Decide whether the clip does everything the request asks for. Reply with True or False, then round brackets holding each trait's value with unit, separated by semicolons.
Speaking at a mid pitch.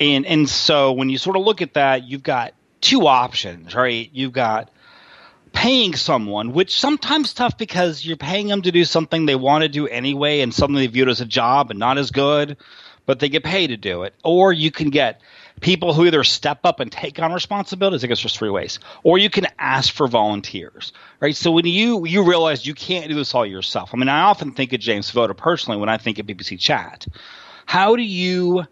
True (145 Hz)